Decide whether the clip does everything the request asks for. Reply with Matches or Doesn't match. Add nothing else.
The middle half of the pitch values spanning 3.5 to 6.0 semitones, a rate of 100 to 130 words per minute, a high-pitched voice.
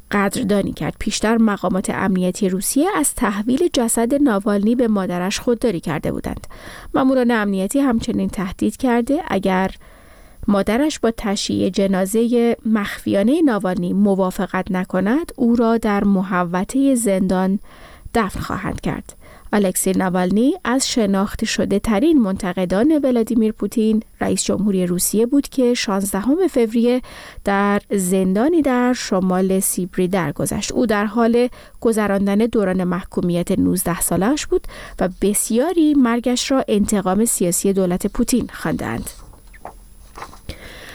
Matches